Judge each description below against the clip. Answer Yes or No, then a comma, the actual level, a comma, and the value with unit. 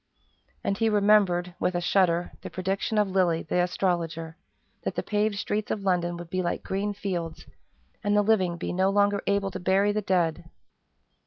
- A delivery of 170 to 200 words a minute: Yes, average, 180 wpm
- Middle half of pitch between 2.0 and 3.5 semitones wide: Yes, average, 2.7 semitones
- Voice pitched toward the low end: No, high, 190 Hz